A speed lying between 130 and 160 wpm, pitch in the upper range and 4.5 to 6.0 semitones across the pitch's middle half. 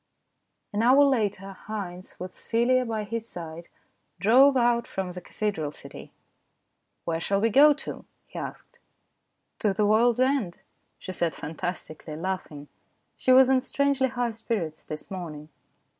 Yes: average, 155 wpm; high, 210 Hz; wide, 5.6 semitones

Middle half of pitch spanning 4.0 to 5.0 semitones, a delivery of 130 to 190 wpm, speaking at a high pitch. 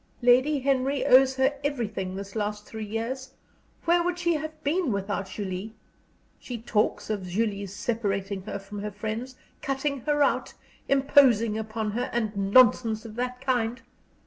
Yes: average, 4.3 semitones; average, 150 wpm; high, 230 Hz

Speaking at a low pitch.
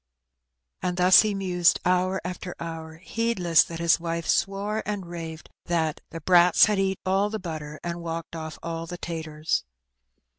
No: medium, 175 Hz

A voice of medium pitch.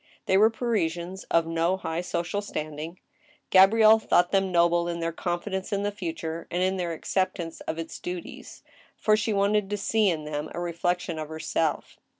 Yes: medium, 175 Hz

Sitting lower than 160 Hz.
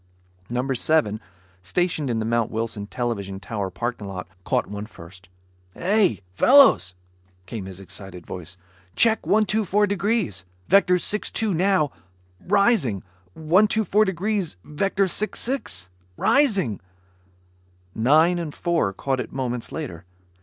Yes: low, 135 Hz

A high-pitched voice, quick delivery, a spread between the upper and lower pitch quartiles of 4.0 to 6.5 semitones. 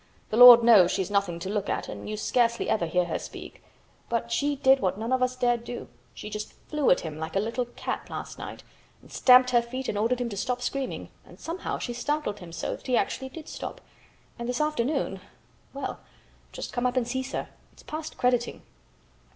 No: high, 240 Hz; fast, 210 wpm; average, 3.6 semitones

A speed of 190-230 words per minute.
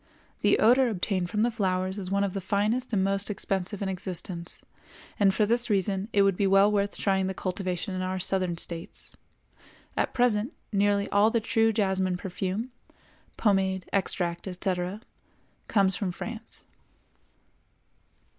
No: average, 150 wpm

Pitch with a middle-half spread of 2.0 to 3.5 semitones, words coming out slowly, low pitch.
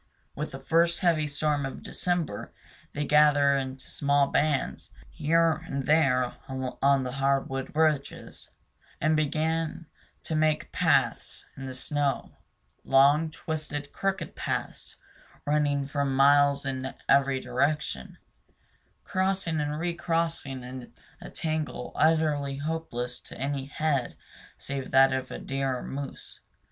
No: narrow, 2.5 semitones; slow, 125 wpm; medium, 145 Hz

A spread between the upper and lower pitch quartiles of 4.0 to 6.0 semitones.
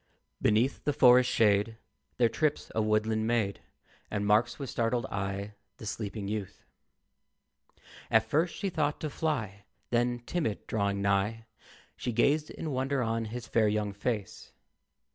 No: average, 3.4 semitones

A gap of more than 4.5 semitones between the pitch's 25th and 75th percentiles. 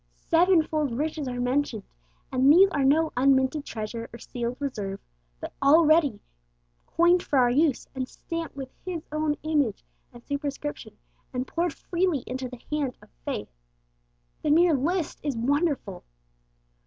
No: average, 3.9 semitones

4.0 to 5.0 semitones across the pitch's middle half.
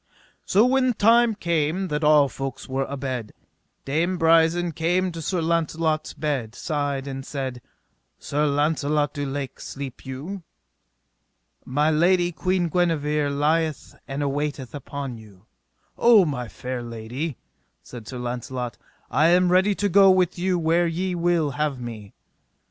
Yes: average, 4.5 semitones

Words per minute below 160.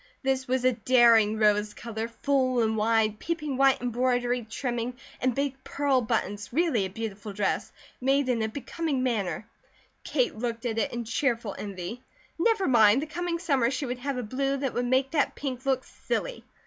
No: average, 180 wpm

